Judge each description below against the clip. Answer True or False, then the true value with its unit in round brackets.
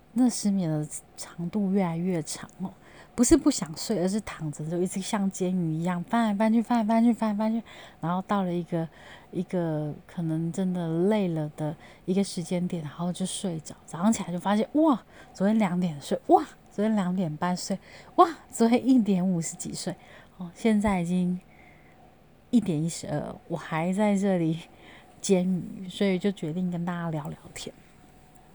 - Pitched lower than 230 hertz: True (185 Hz)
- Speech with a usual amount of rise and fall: True (3.7 semitones)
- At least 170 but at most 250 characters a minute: False (260 characters per minute)